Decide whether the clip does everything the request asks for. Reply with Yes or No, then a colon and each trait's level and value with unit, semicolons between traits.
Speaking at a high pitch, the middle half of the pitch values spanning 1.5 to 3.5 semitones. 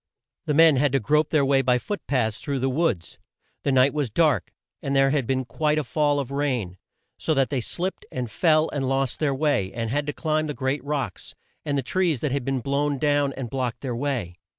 No: medium, 140 Hz; narrow, 2.6 semitones